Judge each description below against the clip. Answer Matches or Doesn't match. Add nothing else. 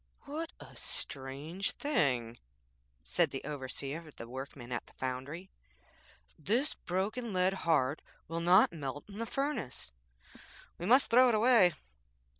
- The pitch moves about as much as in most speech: Doesn't match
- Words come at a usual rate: Doesn't match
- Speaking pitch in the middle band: Matches